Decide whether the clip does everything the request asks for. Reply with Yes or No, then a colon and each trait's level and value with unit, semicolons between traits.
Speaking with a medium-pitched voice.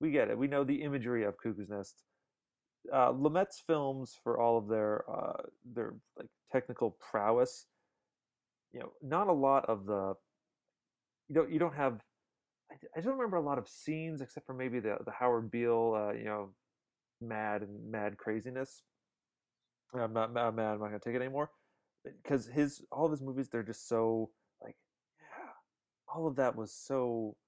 No: low, 120 Hz